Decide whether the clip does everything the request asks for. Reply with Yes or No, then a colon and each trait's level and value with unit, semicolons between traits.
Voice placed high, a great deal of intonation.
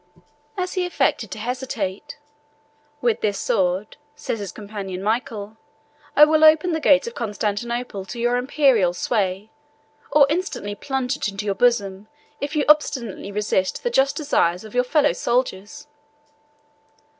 Yes: high, 235 Hz; wide, 6.0 semitones